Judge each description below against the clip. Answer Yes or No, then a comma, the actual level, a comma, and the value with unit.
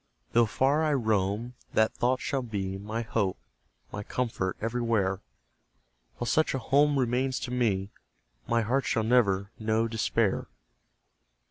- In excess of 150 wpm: No, slow, 135 wpm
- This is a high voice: No, low, 115 Hz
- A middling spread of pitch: Yes, average, 3.4 semitones